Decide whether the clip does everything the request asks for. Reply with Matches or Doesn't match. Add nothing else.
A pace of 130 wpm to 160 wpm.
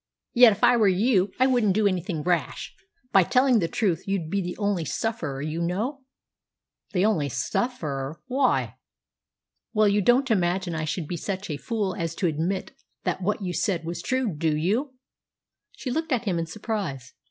Doesn't match